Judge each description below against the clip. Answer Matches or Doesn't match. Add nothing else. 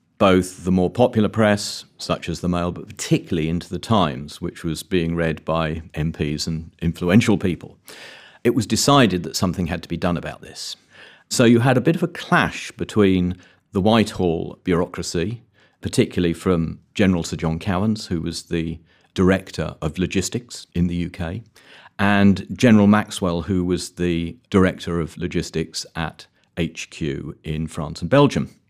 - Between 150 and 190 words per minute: Matches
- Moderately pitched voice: Doesn't match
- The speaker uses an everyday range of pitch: Matches